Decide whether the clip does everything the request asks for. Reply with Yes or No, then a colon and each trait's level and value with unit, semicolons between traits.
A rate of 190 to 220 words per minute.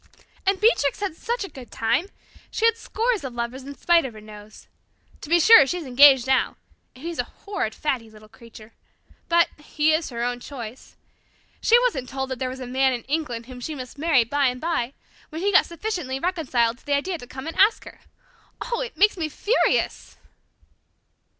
Yes: average, 200 wpm